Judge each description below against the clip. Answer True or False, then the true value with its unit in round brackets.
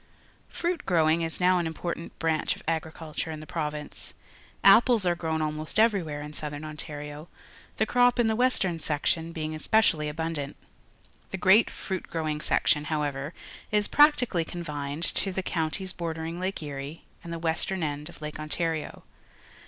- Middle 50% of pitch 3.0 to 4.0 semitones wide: True (3.4 semitones)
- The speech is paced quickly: False (160 wpm)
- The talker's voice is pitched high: False (160 Hz)